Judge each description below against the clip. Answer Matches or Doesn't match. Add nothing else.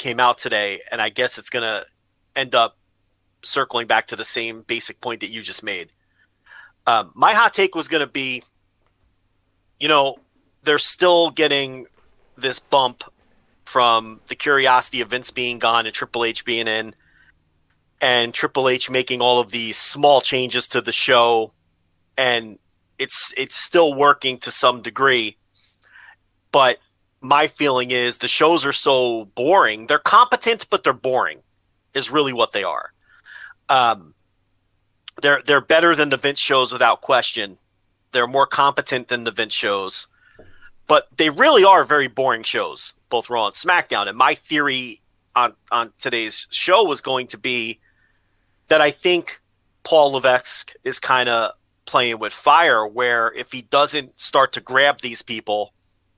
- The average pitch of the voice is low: Matches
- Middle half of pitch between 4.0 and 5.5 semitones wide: Matches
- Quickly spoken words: Doesn't match